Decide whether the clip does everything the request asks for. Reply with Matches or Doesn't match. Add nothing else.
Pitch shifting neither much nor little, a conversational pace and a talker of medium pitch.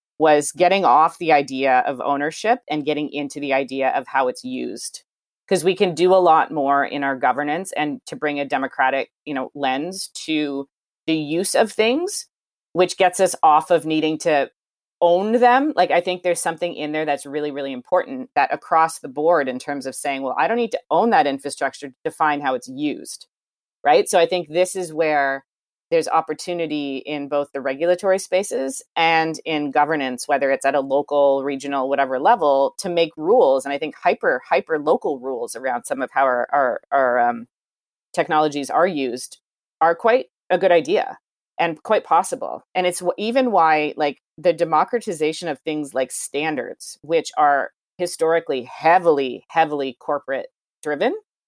Matches